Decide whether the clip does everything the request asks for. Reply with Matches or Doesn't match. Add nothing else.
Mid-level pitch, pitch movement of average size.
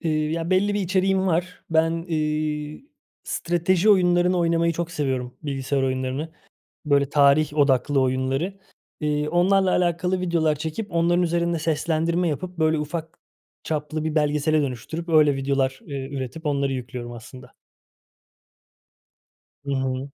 Matches